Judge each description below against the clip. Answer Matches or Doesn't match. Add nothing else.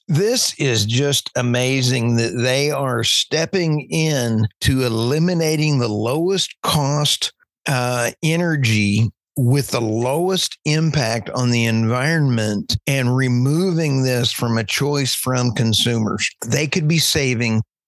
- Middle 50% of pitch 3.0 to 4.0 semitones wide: Doesn't match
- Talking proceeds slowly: Matches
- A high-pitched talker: Doesn't match